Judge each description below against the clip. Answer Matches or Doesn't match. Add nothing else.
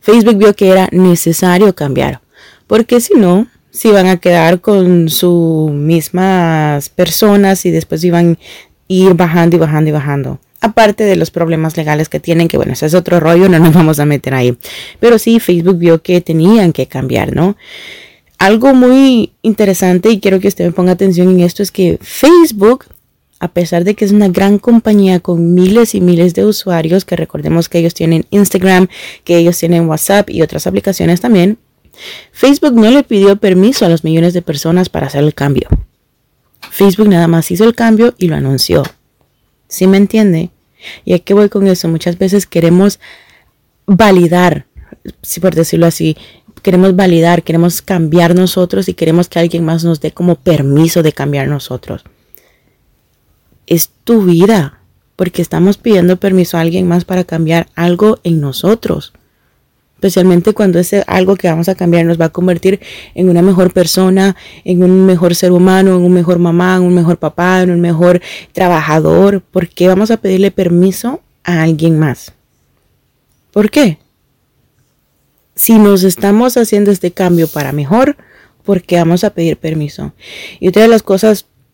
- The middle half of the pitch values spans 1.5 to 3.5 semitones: Matches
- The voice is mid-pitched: Matches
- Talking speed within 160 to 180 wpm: Matches